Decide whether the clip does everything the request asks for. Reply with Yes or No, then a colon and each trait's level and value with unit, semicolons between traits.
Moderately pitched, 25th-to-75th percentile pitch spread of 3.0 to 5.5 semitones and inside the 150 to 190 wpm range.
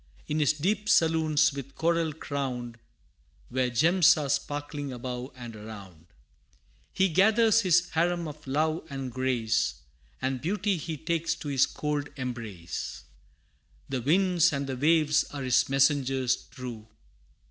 No: medium, 145 Hz; average, 4.3 semitones; slow, 135 wpm